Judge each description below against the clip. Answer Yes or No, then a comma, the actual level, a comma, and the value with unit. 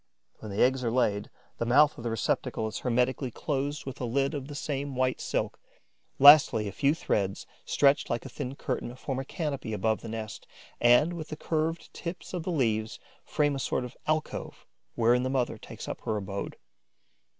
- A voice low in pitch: Yes, low, 130 Hz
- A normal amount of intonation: Yes, average, 4.2 semitones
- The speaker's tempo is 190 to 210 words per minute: Yes, average, 195 wpm